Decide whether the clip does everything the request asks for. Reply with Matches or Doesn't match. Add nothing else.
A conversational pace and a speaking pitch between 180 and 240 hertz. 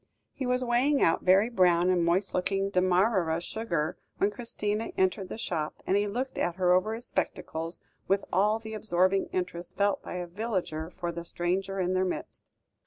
Matches